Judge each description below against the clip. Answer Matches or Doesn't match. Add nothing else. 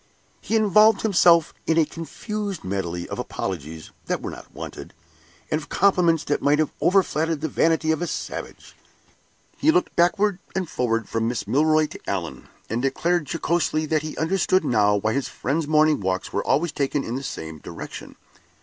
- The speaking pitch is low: Doesn't match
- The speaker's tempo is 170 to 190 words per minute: Matches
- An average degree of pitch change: Doesn't match